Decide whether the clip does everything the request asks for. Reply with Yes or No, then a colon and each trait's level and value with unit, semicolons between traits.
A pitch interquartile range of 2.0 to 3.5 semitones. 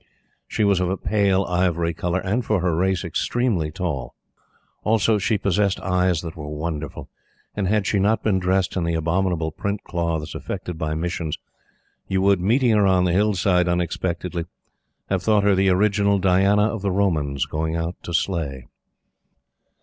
Yes: average, 3.1 semitones